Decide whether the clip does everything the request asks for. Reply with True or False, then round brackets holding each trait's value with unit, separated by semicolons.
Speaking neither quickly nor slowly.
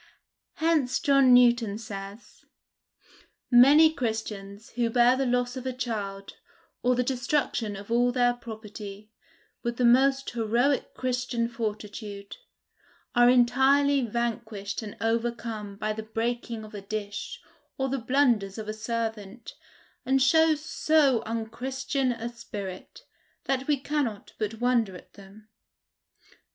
False (125 wpm)